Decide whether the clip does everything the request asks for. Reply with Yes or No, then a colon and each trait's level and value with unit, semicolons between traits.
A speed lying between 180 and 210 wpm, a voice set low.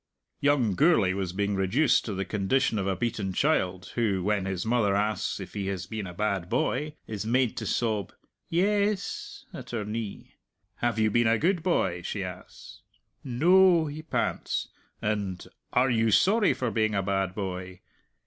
No: average, 170 wpm; low, 110 Hz